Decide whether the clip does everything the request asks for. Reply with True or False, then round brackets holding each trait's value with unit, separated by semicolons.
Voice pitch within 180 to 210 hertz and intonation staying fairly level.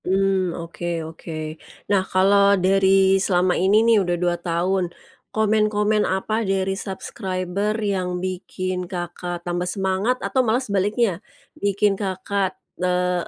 True (190 Hz; 1.9 semitones)